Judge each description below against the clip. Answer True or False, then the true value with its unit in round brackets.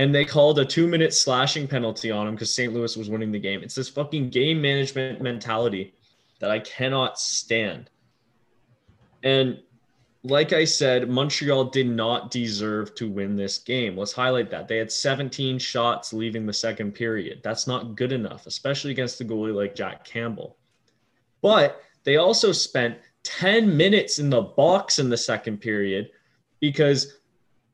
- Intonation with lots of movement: False (3.6 semitones)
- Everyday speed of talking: True (160 wpm)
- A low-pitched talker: True (125 Hz)